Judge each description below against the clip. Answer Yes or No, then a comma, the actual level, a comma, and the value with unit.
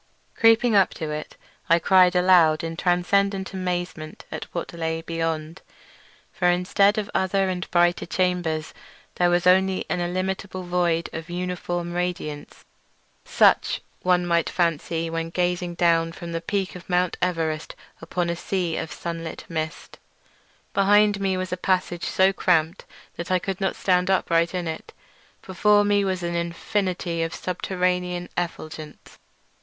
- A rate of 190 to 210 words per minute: No, average, 150 wpm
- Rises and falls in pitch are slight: Yes, narrow, 1.9 semitones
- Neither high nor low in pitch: Yes, medium, 175 Hz